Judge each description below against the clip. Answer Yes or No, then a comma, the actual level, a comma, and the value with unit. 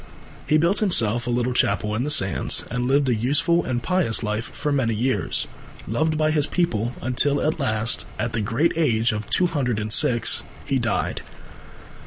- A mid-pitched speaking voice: No, low, 125 Hz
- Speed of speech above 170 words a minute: Yes, average, 185 wpm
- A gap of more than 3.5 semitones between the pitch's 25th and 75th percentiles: Yes, average, 5.1 semitones